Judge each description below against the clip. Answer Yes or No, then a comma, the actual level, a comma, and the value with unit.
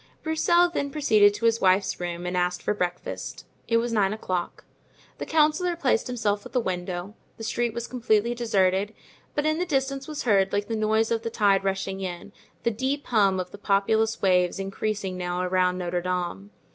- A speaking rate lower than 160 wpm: No, average, 190 wpm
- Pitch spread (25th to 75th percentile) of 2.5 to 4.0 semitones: No, average, 4.4 semitones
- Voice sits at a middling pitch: No, high, 205 Hz